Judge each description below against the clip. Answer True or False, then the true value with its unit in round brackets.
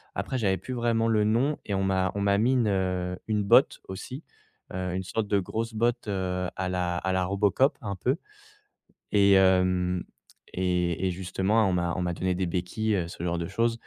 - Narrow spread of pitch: False (3.1 semitones)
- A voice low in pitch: True (95 Hz)